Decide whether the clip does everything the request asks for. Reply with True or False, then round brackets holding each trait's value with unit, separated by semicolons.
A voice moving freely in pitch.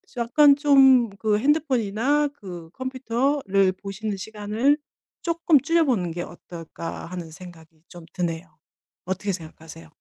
True (7.5 semitones)